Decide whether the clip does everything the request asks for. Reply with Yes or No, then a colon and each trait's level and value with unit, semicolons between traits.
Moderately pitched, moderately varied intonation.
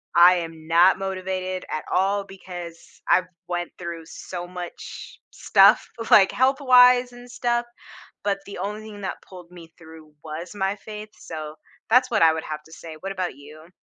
Yes: medium, 180 Hz; average, 3.7 semitones